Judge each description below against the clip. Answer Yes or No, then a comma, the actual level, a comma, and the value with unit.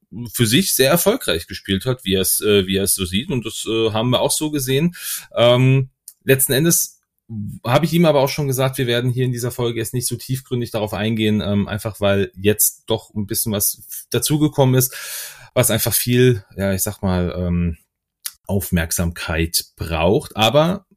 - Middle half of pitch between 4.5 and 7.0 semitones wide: Yes, average, 4.8 semitones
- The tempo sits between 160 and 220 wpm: Yes, average, 185 wpm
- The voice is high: No, low, 120 Hz